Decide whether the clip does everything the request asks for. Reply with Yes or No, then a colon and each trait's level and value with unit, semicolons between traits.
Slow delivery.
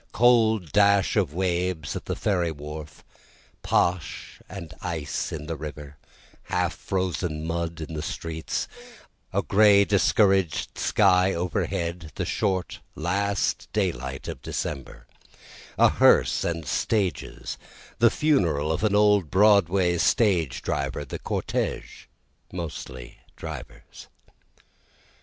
Yes: slow, 110 wpm